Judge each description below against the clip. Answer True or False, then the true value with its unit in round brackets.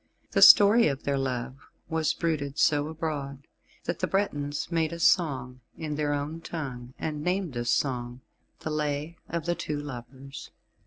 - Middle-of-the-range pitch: True (145 Hz)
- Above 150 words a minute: True (160 wpm)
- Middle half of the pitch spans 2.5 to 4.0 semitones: True (3.1 semitones)